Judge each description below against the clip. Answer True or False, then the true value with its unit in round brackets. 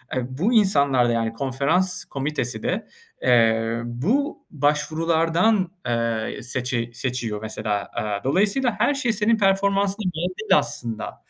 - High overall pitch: False (145 Hz)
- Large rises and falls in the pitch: True (8.6 semitones)